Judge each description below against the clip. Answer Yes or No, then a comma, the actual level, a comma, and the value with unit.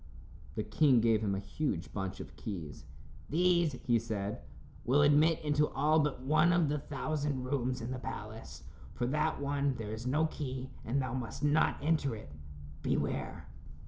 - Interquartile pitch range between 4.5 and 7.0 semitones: Yes, average, 5.0 semitones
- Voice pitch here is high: No, low, 130 Hz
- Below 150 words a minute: No, average, 170 wpm